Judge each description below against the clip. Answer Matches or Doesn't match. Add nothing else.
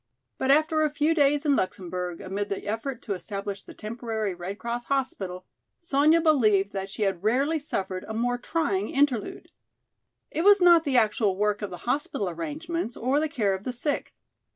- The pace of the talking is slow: Doesn't match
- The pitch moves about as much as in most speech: Doesn't match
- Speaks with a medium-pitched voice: Doesn't match